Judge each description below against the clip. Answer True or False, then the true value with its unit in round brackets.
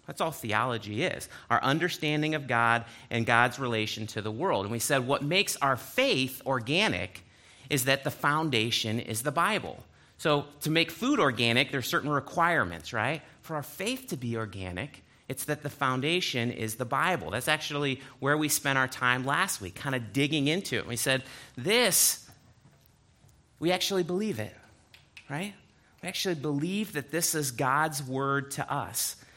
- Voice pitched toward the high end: False (140 Hz)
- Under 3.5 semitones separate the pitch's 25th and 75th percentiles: False (4.7 semitones)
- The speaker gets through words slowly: False (170 wpm)